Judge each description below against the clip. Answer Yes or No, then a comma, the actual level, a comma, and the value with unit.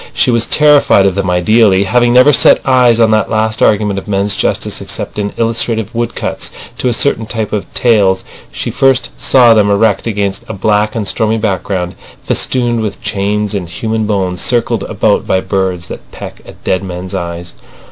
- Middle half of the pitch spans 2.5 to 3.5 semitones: Yes, average, 3.0 semitones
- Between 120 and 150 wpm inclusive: No, average, 180 wpm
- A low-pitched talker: Yes, low, 105 Hz